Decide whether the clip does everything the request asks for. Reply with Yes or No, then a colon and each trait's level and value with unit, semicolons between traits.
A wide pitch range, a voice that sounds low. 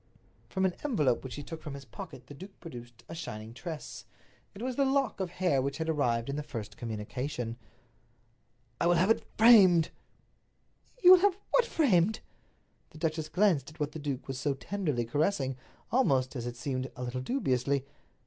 No: wide, 6.6 semitones; medium, 150 Hz